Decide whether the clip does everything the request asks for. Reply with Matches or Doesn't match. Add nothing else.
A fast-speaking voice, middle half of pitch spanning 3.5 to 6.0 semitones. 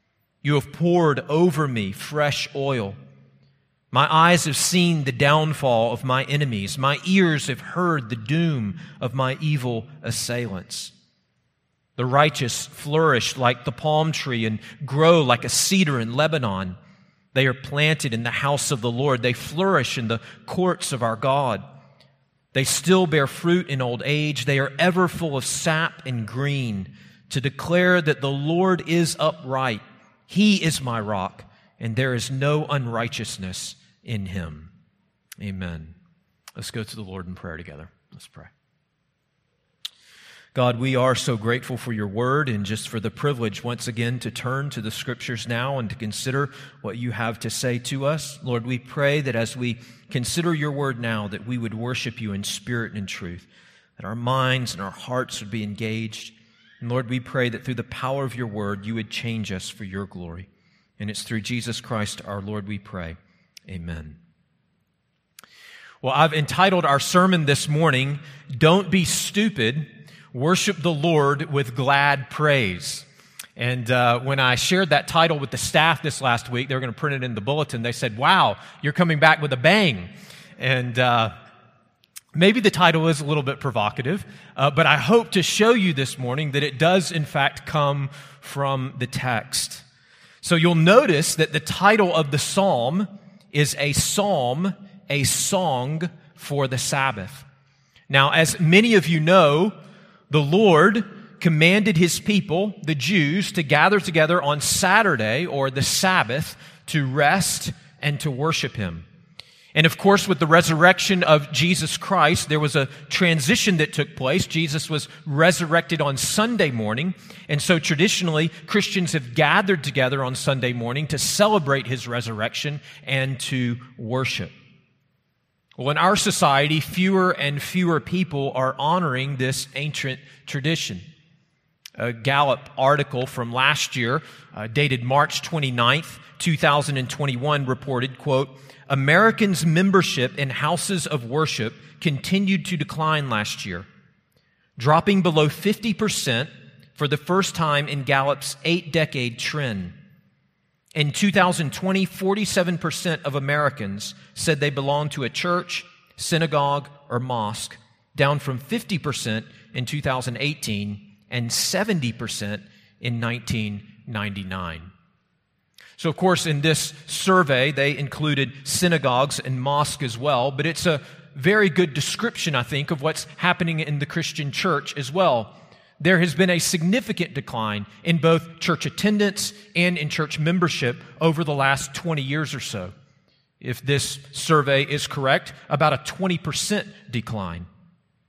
Doesn't match